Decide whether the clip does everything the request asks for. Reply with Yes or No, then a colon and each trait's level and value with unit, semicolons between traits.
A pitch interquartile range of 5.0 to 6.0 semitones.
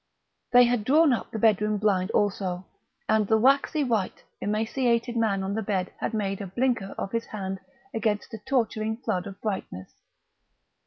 No: average, 3.1 semitones